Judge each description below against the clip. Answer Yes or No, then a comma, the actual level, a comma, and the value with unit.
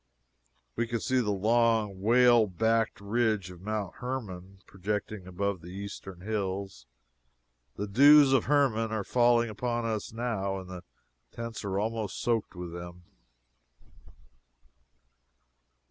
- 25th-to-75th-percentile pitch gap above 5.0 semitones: No, average, 3.4 semitones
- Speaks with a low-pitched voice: Yes, low, 105 Hz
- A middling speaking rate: No, slow, 125 wpm